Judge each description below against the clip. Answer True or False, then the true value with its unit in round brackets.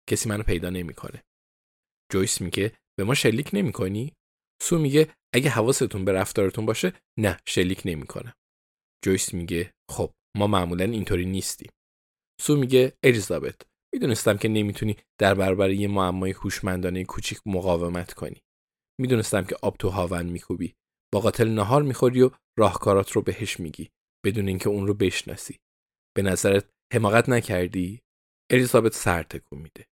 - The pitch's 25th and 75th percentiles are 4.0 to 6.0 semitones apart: False (3.6 semitones)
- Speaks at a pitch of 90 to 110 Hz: True (100 Hz)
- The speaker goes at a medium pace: True (135 wpm)